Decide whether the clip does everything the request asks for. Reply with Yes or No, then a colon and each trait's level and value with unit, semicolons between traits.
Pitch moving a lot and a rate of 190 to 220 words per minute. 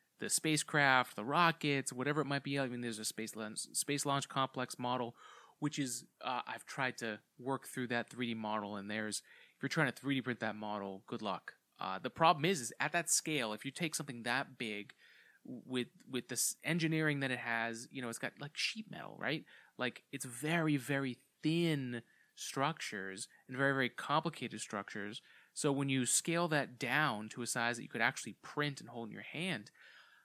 No: average, 4.0 semitones; average, 200 wpm